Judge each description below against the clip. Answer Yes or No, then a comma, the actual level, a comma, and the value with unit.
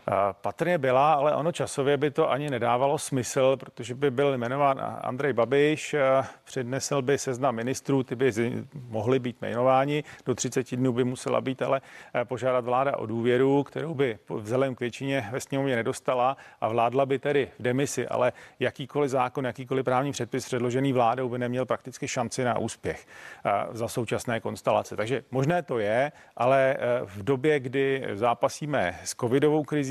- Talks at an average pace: Yes, average, 160 wpm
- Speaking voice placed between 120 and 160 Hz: Yes, low, 130 Hz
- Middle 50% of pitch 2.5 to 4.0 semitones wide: No, narrow, 2.1 semitones